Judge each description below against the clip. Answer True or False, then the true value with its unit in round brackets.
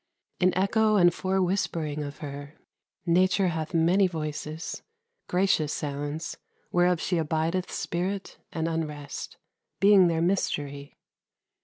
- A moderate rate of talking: False (110 wpm)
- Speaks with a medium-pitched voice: True (165 Hz)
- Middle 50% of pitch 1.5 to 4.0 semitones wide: True (3.5 semitones)